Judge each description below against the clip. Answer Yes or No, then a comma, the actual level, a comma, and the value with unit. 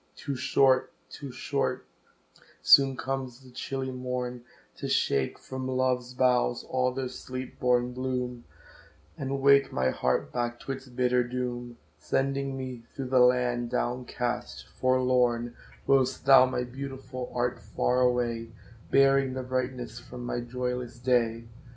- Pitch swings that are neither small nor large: No, narrow, 1.2 semitones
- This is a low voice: Yes, low, 125 Hz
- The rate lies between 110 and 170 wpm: Yes, average, 140 wpm